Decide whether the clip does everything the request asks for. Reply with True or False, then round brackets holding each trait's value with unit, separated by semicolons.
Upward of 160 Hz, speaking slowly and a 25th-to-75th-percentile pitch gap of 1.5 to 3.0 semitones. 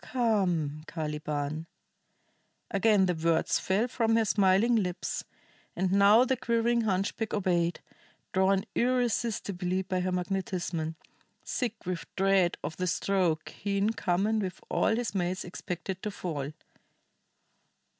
False (190 Hz; 125 wpm; 3.7 semitones)